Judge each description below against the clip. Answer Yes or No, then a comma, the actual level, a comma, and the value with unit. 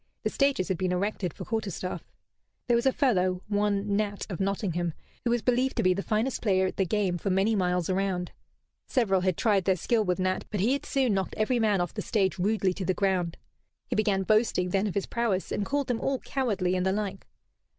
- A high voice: Yes, high, 195 Hz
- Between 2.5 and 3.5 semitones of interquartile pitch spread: Yes, average, 2.9 semitones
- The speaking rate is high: Yes, fast, 235 wpm